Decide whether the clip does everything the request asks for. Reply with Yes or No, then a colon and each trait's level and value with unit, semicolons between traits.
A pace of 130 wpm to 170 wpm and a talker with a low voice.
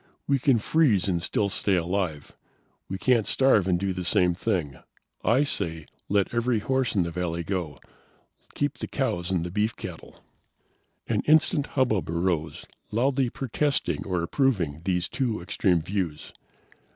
Yes: average, 150 wpm; very low, 95 Hz